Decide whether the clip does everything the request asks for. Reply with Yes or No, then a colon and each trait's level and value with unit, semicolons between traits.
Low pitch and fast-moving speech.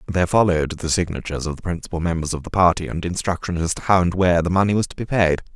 Yes: very low, 85 Hz; fast, 260 wpm